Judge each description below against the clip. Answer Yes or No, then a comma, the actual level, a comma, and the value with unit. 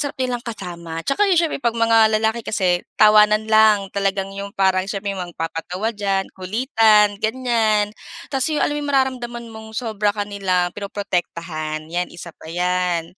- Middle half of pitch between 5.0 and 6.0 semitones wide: No, average, 3.9 semitones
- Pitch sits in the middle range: No, high, 210 Hz